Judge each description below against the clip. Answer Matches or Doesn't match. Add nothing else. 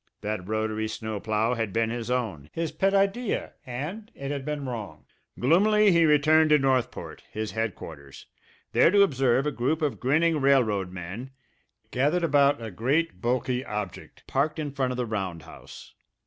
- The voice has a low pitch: Matches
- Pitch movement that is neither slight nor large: Doesn't match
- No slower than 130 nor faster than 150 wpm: Doesn't match